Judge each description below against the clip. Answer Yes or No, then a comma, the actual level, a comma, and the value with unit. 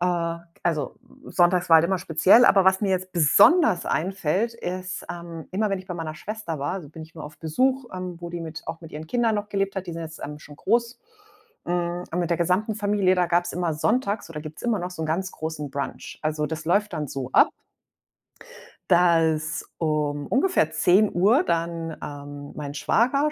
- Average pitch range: Yes, average, 3.6 semitones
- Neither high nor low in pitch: Yes, medium, 175 Hz